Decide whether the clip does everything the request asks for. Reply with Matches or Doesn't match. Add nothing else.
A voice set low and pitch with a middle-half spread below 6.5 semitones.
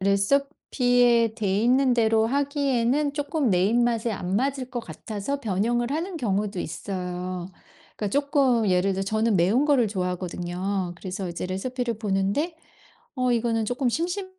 Doesn't match